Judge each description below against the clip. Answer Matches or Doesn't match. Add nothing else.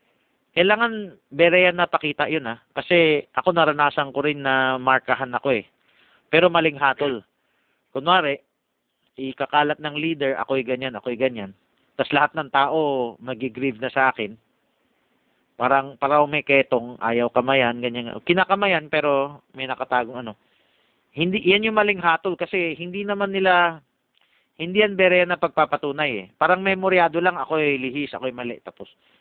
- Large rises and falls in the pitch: Doesn't match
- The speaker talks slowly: Doesn't match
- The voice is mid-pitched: Matches